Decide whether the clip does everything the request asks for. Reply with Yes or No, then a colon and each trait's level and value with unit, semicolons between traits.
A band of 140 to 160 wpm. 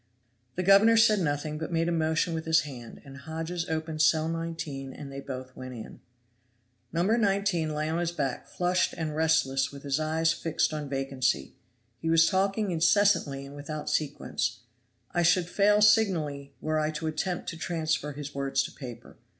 No: average, 175 wpm